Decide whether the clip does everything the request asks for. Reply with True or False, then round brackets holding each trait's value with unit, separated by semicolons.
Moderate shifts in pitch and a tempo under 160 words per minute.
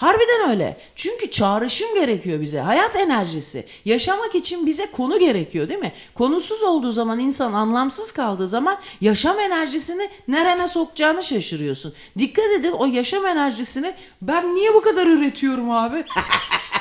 False (8.2 semitones; 135 wpm)